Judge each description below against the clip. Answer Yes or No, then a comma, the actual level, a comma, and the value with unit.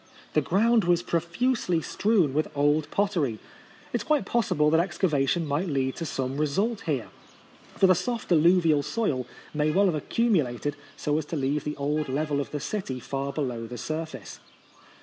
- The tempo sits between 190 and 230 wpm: No, average, 180 wpm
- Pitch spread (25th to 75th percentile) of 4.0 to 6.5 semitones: Yes, average, 4.6 semitones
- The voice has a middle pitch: Yes, medium, 155 Hz